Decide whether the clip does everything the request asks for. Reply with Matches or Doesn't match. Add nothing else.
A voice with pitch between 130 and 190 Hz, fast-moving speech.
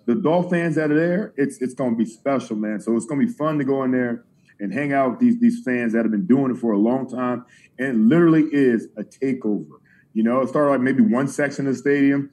Matches